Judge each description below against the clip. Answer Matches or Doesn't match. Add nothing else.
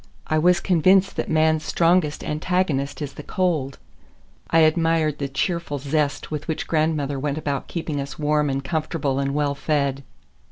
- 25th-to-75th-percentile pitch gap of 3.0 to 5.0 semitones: Doesn't match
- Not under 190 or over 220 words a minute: Doesn't match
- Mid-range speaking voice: Matches